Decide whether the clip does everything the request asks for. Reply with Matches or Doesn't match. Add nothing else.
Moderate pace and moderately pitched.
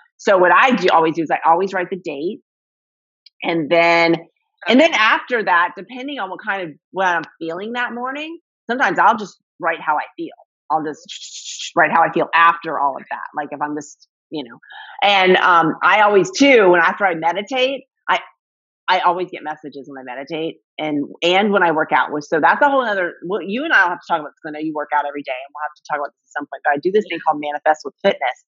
Doesn't match